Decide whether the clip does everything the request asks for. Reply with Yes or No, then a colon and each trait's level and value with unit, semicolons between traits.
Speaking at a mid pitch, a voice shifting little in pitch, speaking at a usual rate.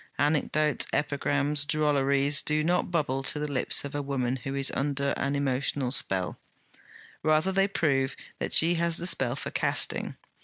Yes: medium, 145 Hz; narrow, 2.0 semitones; average, 160 wpm